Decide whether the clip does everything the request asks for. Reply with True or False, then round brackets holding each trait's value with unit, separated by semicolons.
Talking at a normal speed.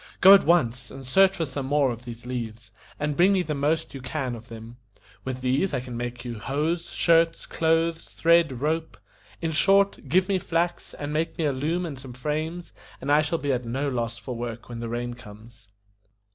False (210 wpm)